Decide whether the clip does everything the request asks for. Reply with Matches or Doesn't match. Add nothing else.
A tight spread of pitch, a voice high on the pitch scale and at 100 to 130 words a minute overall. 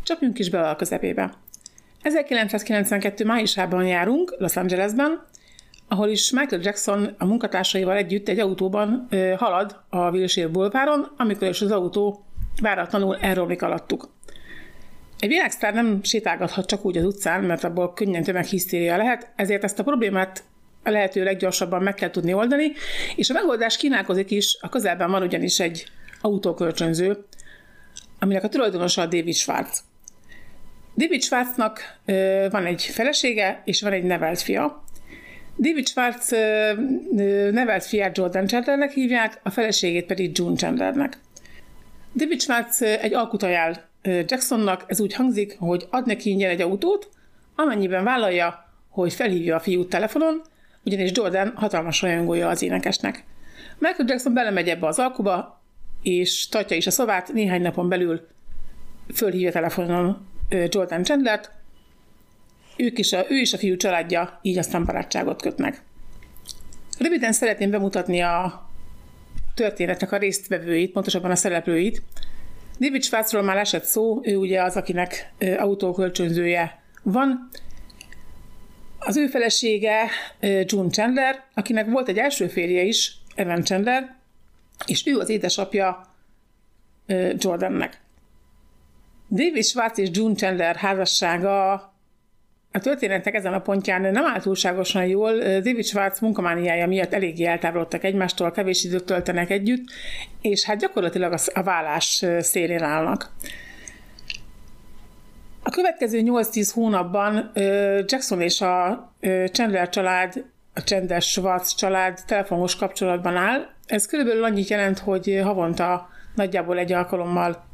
Doesn't match